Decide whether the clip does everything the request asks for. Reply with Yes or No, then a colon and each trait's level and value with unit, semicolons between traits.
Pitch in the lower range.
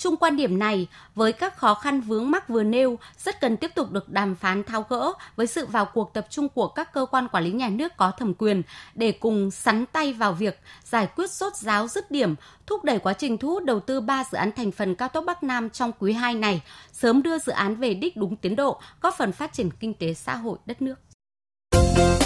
No: high, 225 Hz